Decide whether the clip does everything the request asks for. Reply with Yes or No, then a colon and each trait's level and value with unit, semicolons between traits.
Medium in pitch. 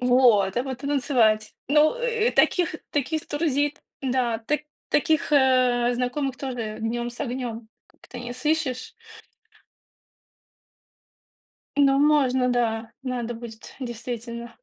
No: very high, 250 Hz